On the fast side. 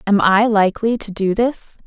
No: average, 195 wpm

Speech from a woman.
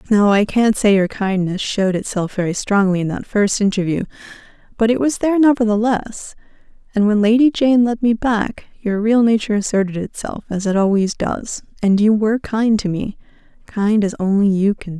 Yes: female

